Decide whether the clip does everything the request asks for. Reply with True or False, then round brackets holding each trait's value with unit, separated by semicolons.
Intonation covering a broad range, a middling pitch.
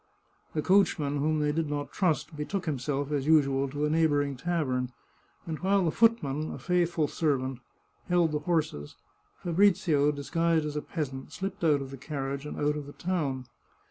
False (3.1 semitones; 150 Hz)